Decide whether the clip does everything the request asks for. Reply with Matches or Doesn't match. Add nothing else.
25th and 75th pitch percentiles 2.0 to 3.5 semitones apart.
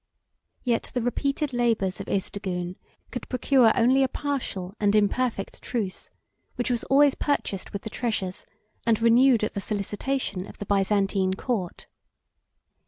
Doesn't match